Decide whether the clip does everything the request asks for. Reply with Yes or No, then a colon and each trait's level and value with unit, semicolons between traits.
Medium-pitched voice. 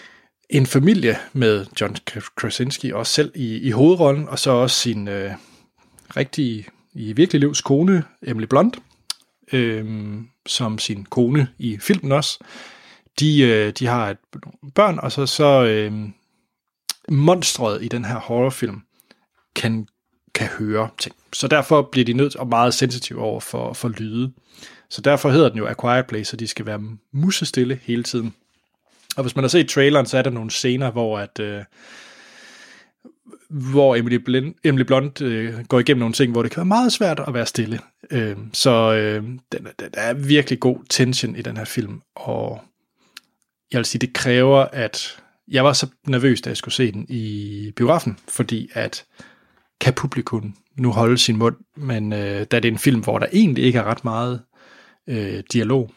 No: low, 125 Hz